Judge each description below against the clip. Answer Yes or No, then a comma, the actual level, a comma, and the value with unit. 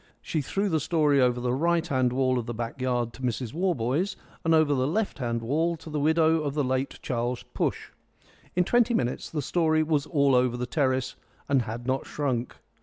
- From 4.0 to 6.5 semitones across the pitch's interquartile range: Yes, average, 4.3 semitones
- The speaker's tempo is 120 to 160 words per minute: No, fast, 205 wpm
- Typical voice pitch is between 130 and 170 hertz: Yes, medium, 140 Hz